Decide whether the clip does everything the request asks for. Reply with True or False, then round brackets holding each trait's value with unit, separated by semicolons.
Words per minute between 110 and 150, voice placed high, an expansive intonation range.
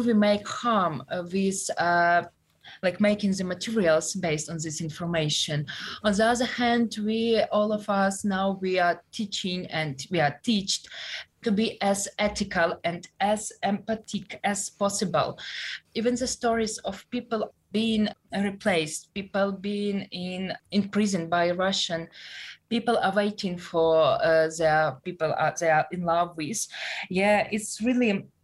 False (145 wpm; 195 Hz; 3.7 semitones)